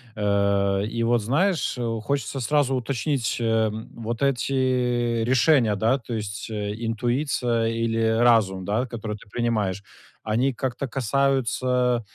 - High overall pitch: No, low, 120 Hz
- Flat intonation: No, average, 3.0 semitones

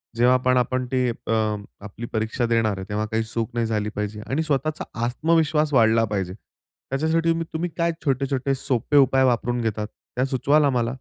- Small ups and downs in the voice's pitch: No, average, 3.7 semitones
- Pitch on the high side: No, low, 125 Hz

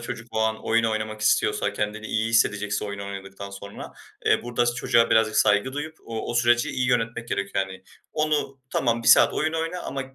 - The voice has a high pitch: No, low, 115 Hz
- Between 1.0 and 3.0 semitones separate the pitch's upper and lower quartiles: Yes, narrow, 2.6 semitones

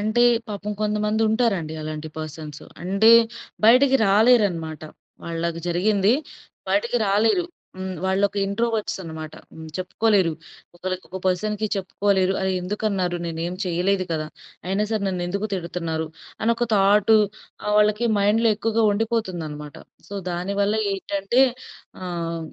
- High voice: Yes, high, 195 Hz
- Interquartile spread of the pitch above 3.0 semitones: Yes, average, 3.6 semitones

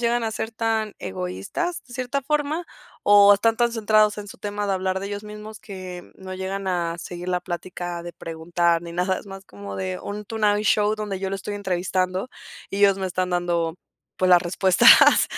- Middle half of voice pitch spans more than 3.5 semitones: No, average, 3.2 semitones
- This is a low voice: No, high, 195 Hz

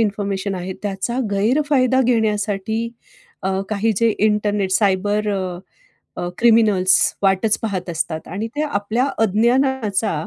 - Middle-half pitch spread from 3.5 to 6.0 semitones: No, average, 2.8 semitones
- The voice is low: No, high, 210 Hz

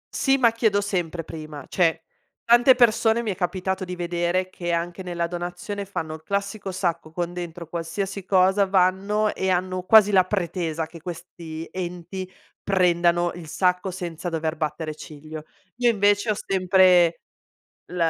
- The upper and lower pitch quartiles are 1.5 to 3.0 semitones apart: Yes, narrow, 2.6 semitones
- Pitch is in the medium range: Yes, medium, 180 Hz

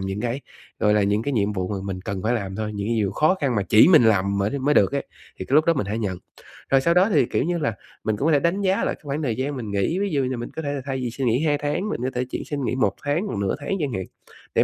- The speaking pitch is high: No, low, 125 Hz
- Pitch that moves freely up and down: Yes, wide, 6.1 semitones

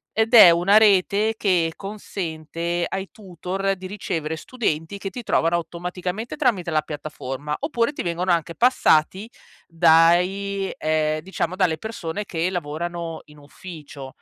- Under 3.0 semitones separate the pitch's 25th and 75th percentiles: No, average, 3.5 semitones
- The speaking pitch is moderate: Yes, medium, 175 Hz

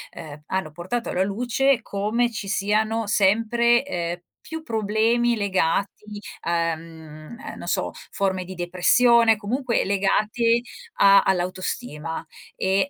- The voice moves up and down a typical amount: Yes, average, 4.5 semitones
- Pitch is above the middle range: Yes, high, 205 Hz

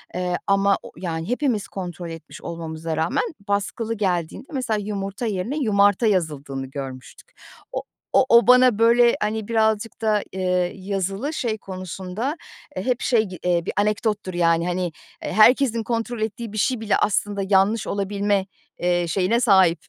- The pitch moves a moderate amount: Yes, average, 3.9 semitones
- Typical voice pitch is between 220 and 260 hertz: No, high, 200 Hz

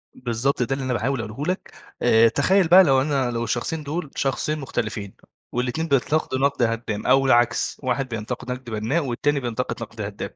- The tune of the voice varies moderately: Yes, average, 3.2 semitones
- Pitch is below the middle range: Yes, low, 125 Hz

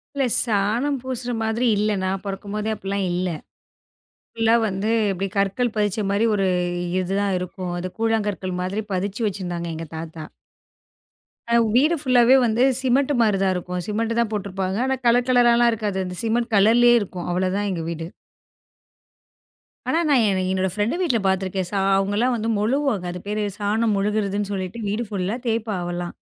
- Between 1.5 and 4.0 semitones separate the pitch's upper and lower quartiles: Yes, average, 3.5 semitones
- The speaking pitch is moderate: No, high, 205 Hz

